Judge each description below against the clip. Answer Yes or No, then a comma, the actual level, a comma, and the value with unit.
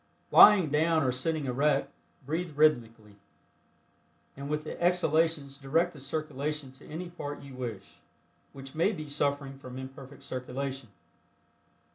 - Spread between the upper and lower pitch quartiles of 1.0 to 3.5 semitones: Yes, average, 2.9 semitones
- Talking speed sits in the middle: No, slow, 130 wpm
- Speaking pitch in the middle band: Yes, medium, 145 Hz